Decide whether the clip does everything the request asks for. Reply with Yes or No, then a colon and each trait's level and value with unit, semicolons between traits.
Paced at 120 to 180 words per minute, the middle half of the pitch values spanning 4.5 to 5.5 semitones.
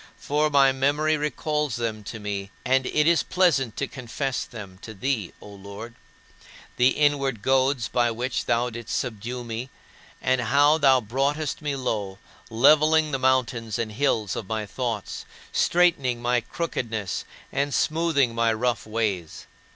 No: average, 150 wpm; average, 4.0 semitones